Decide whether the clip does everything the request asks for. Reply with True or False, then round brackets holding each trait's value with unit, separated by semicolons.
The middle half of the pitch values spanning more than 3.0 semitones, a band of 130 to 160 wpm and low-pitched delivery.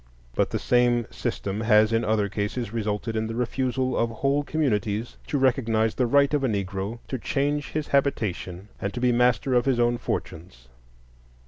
False (3.6 semitones; 180 wpm; 120 Hz)